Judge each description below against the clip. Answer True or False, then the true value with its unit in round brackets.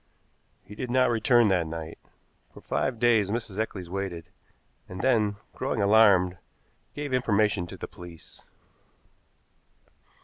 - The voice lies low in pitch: True (105 Hz)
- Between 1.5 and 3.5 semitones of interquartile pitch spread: False (4.7 semitones)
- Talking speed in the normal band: False (125 wpm)